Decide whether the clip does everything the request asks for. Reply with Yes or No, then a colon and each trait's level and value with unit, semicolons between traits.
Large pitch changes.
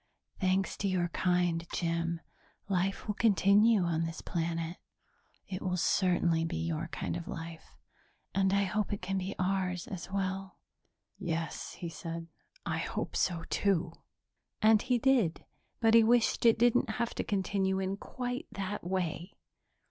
No: average, 3.1 semitones